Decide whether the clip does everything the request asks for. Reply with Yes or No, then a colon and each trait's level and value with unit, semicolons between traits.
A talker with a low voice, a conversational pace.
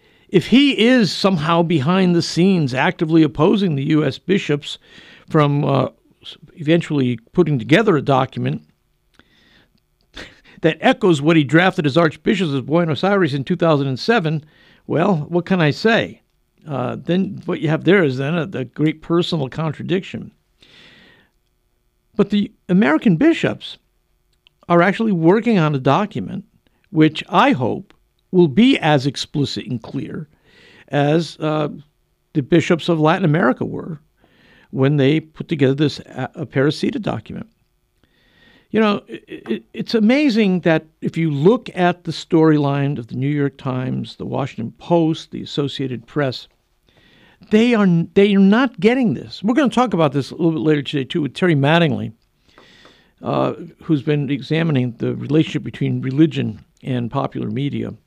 No: medium, 160 Hz; average, 145 wpm